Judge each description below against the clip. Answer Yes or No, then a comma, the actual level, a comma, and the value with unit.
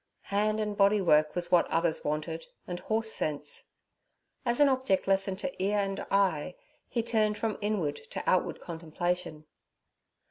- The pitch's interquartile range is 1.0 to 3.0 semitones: No, average, 4.3 semitones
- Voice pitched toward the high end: Yes, high, 195 Hz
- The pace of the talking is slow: No, average, 150 wpm